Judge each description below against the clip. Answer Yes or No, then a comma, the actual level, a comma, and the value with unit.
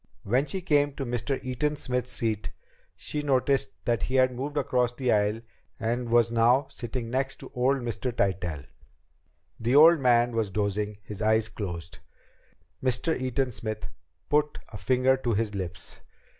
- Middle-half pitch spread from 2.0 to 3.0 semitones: No, average, 3.5 semitones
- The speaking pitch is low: Yes, low, 120 Hz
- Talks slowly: No, average, 155 wpm